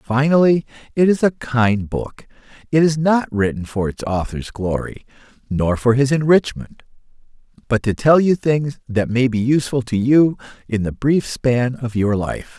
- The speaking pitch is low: Yes, low, 130 Hz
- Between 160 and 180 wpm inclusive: Yes, average, 170 wpm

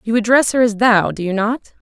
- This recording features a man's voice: No, female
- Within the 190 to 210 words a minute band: No, fast, 255 wpm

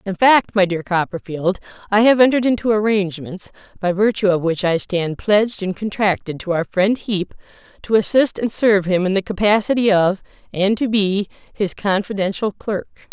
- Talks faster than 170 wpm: No, average, 165 wpm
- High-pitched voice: Yes, high, 200 Hz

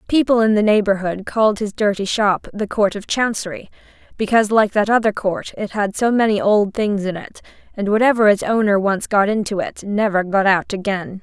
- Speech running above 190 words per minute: Yes, average, 200 wpm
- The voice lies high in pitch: Yes, high, 205 Hz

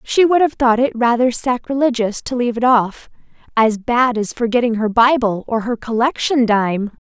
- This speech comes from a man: No, female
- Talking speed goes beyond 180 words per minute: No, average, 170 wpm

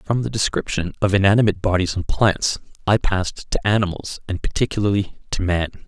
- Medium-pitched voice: No, low, 100 Hz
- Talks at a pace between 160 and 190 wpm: Yes, average, 165 wpm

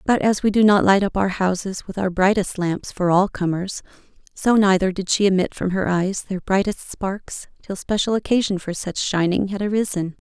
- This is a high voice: Yes, high, 195 Hz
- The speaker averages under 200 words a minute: No, fast, 205 wpm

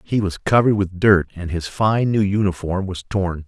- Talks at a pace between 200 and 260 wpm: Yes, fast, 205 wpm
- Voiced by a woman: No, male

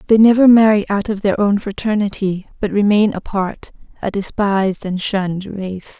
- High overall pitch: Yes, high, 200 Hz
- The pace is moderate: Yes, average, 160 wpm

